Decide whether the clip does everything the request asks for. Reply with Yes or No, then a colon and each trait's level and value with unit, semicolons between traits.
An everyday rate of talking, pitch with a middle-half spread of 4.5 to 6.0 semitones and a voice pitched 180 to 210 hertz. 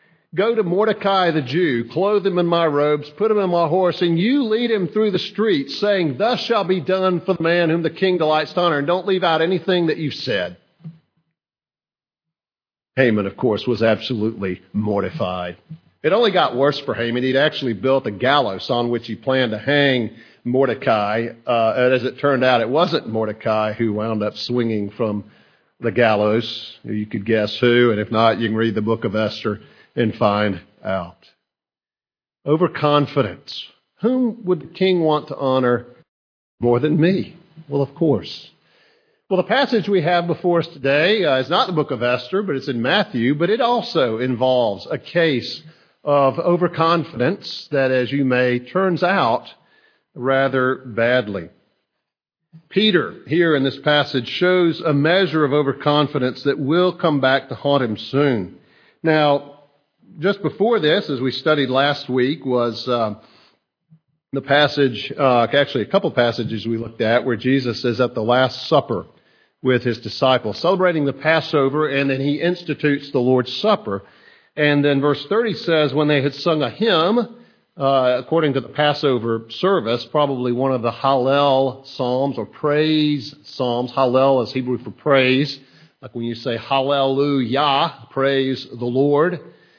No: average, 165 wpm; average, 5.2 semitones; medium, 140 Hz